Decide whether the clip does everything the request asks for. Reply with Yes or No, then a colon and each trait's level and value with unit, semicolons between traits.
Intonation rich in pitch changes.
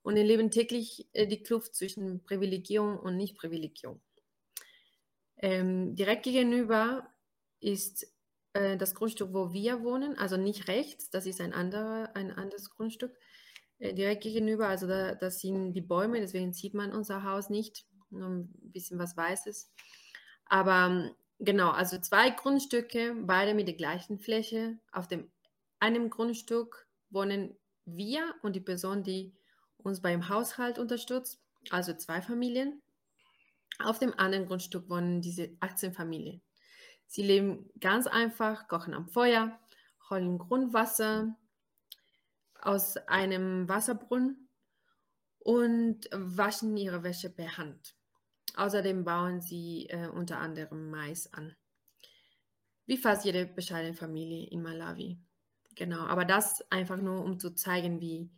No: average, 3.6 semitones